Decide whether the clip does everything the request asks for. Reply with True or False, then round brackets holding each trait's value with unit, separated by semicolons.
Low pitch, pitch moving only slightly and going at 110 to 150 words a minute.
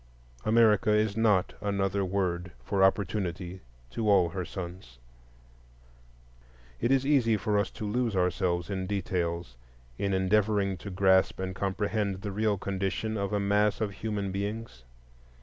True (100 Hz; 2.1 semitones; 140 wpm)